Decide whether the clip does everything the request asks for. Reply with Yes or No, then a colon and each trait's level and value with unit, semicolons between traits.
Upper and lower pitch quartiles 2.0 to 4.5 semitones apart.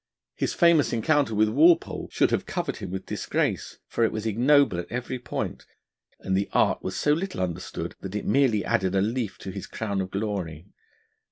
No: wide, 5.4 semitones